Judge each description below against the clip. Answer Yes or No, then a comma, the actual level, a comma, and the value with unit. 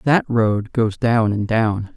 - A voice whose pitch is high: No, low, 110 Hz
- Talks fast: No, average, 185 wpm